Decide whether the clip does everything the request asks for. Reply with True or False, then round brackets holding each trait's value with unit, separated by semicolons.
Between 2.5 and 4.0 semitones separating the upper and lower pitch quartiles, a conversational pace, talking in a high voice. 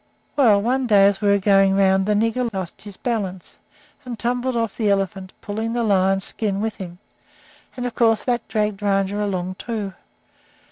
True (2.8 semitones; 180 wpm; 205 Hz)